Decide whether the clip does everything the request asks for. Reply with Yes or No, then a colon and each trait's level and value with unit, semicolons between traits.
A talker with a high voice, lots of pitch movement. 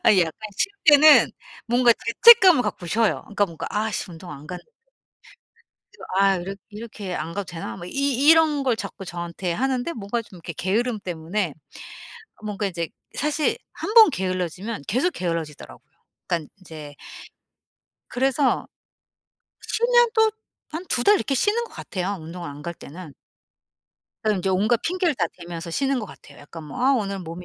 Yes: high, 200 Hz; wide, 7.6 semitones